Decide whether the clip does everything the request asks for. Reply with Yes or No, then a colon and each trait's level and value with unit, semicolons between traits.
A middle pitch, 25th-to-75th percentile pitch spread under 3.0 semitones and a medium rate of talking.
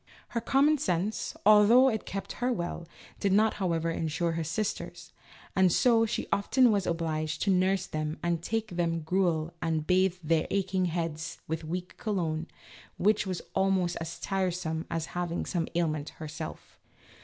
No: medium, 175 Hz; average, 3.3 semitones; average, 160 wpm